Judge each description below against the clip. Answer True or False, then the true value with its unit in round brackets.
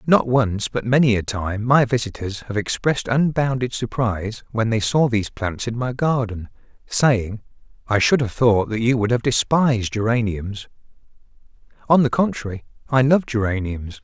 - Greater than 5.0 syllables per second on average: False (4.8 syllables/s)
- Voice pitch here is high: False (115 Hz)